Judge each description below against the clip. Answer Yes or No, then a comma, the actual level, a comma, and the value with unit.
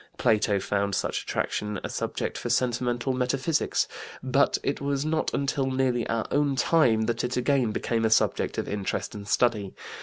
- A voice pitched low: Yes, low, 120 Hz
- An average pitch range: Yes, average, 3.6 semitones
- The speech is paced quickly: No, average, 170 wpm